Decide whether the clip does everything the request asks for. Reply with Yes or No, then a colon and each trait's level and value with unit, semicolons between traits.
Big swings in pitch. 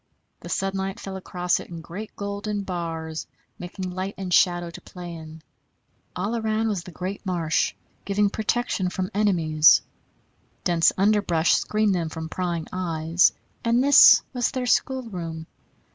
No: average, 3.4 semitones